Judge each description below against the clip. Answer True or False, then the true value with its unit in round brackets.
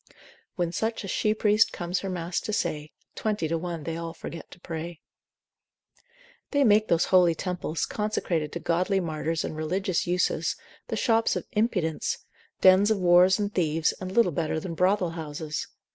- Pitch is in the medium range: True (175 Hz)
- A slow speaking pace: False (170 wpm)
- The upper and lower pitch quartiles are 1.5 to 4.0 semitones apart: True (3.3 semitones)